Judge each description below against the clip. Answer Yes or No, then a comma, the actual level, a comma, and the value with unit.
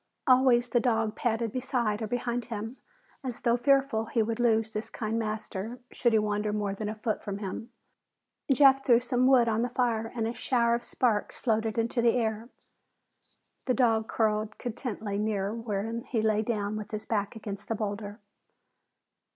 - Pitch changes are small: Yes, narrow, 2.2 semitones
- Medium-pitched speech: No, high, 225 Hz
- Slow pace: No, average, 175 wpm